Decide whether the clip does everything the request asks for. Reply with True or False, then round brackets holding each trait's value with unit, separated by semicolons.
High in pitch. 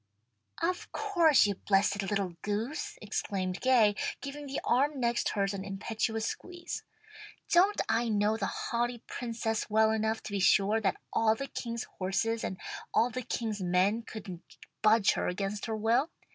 True (220 Hz)